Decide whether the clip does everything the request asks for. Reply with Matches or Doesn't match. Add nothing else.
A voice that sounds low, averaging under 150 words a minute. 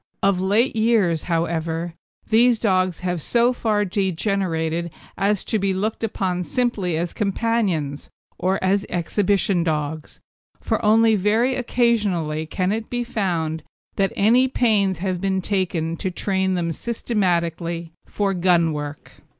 Doesn't match